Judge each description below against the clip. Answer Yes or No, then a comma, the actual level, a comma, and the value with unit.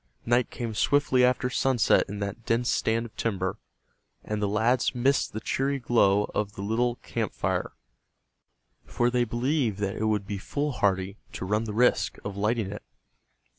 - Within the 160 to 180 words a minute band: Yes, average, 170 wpm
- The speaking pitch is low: Yes, low, 115 Hz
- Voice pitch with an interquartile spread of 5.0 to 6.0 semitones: No, average, 3.3 semitones